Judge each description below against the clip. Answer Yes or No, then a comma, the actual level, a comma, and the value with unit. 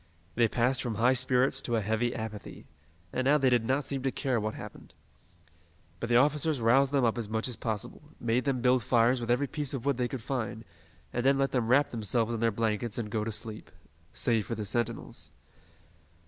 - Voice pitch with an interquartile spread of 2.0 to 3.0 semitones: Yes, narrow, 2.6 semitones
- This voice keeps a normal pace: No, fast, 215 wpm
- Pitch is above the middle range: No, low, 120 Hz